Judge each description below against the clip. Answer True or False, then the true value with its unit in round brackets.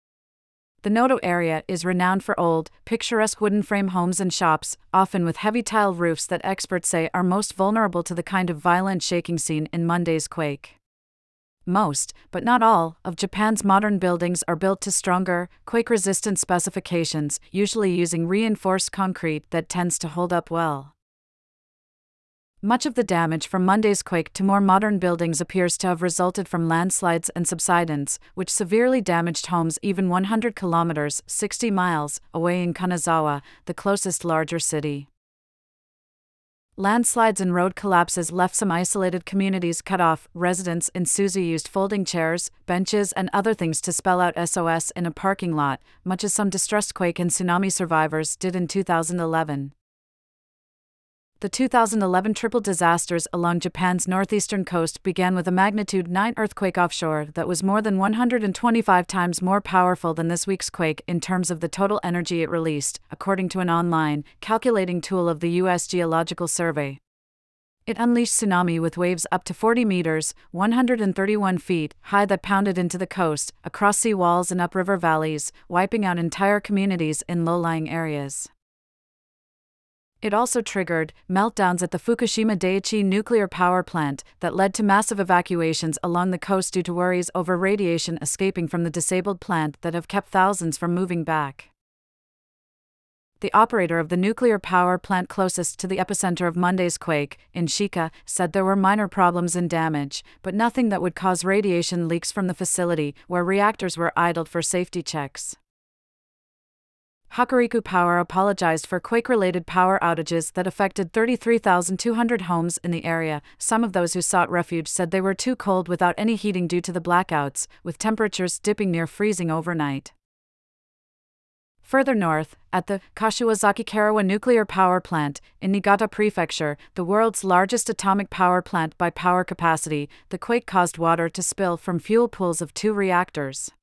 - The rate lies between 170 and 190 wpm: False (160 wpm)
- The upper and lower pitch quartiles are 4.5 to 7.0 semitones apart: False (2.8 semitones)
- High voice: False (180 Hz)